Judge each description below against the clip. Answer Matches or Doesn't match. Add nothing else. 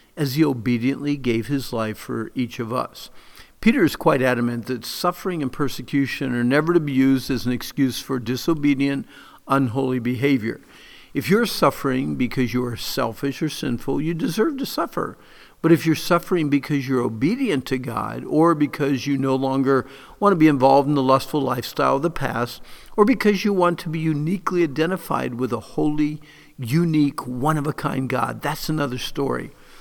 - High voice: Doesn't match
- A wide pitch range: Doesn't match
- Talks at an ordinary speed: Matches